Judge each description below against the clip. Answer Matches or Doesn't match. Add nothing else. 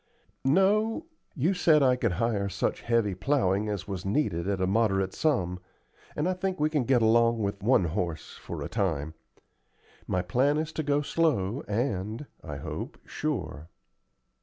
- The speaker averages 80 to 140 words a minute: Doesn't match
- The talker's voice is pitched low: Matches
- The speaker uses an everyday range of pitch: Doesn't match